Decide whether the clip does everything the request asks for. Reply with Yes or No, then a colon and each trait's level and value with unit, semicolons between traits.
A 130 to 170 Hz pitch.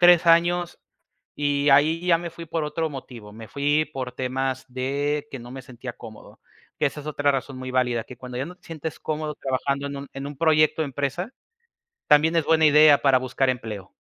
Yes: medium, 140 Hz